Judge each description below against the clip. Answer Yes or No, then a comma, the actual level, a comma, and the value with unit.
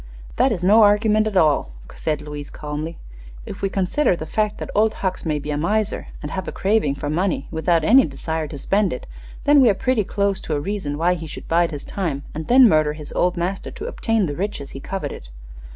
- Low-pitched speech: No, medium, 175 Hz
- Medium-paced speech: No, fast, 225 wpm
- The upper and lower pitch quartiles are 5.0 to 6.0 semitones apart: Yes, wide, 5.4 semitones